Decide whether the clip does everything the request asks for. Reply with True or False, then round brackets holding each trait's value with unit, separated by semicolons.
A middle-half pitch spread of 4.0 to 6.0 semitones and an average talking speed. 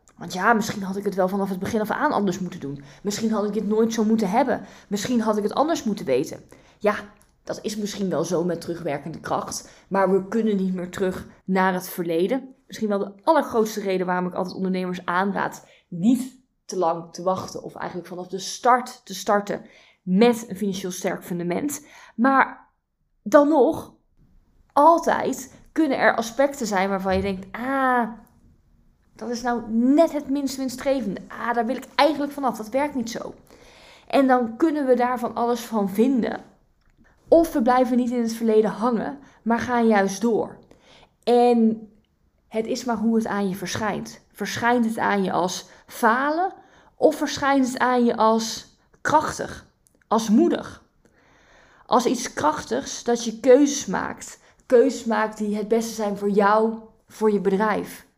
True (4.3 semitones; 170 wpm)